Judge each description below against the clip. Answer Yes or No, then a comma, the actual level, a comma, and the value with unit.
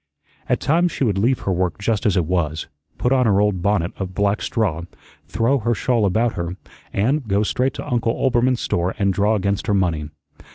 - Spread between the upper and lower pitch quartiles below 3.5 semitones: No, average, 4.3 semitones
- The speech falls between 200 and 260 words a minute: Yes, fast, 205 wpm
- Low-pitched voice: Yes, low, 105 Hz